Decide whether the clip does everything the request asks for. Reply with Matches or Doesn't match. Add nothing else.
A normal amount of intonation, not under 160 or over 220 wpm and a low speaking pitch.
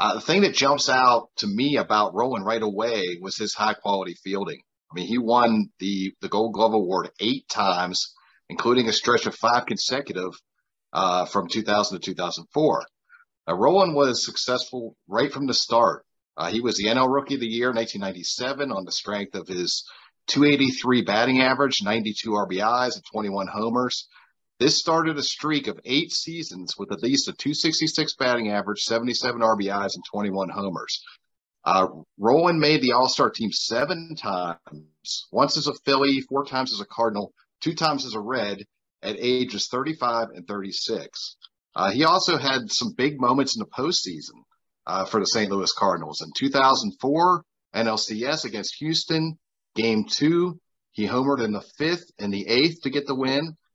Doesn't match